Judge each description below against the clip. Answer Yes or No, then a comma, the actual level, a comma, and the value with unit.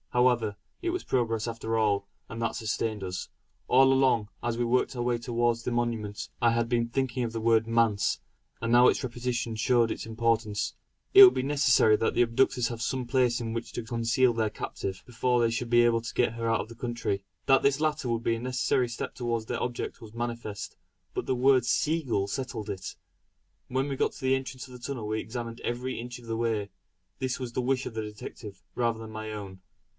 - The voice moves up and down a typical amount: No, narrow, 1.9 semitones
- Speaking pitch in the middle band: No, low, 120 Hz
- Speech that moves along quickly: Yes, fast, 220 wpm